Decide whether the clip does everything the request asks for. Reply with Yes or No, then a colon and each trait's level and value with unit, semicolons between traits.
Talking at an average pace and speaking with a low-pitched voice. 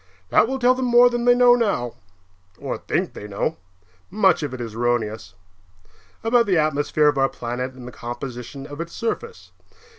No: average, 180 wpm; medium, 145 Hz